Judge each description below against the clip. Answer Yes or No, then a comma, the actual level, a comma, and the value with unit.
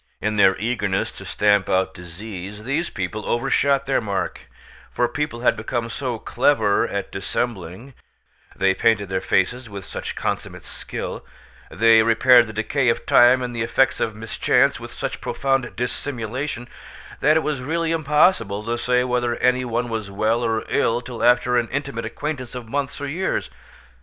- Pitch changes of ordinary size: Yes, average, 3.3 semitones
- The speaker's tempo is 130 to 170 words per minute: Yes, average, 155 wpm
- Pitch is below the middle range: Yes, low, 120 Hz